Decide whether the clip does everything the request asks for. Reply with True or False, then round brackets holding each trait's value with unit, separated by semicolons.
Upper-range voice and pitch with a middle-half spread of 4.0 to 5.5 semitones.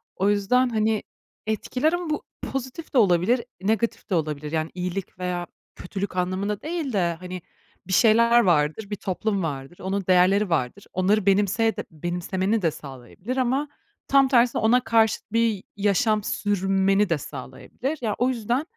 True (200 Hz; 4.3 semitones)